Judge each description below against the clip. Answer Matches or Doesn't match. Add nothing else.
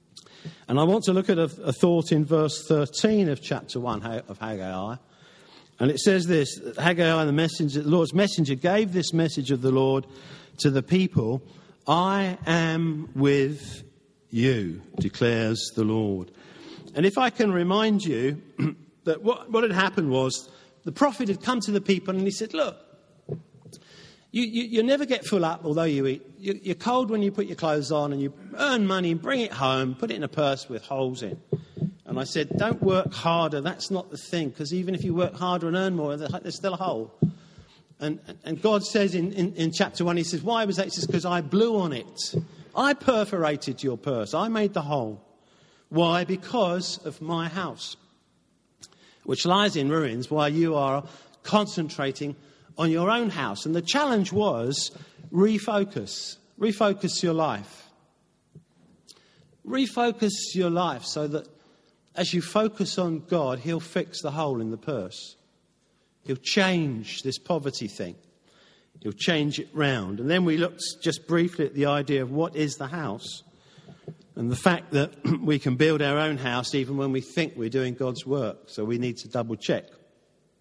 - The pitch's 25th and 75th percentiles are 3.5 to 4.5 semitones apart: Doesn't match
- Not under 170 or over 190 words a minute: Matches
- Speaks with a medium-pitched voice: Matches